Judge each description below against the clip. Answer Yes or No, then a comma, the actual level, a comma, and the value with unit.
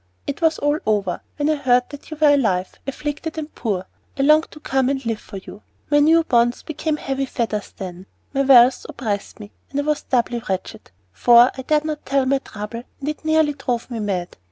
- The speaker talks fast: Yes, fast, 210 wpm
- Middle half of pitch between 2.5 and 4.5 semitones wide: No, average, 4.9 semitones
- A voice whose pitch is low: No, very high, 265 Hz